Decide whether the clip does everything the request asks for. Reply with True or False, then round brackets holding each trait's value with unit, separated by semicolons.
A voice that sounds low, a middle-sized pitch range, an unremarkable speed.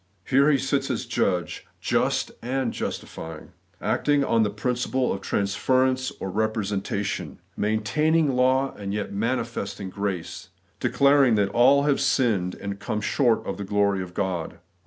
True (110 Hz; 4.8 semitones; 160 wpm)